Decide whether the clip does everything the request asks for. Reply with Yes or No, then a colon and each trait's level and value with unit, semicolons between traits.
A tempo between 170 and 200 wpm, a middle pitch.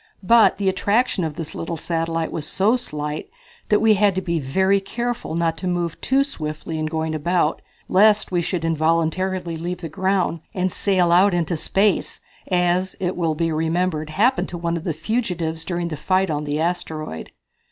Yes: average, 175 wpm; medium, 175 Hz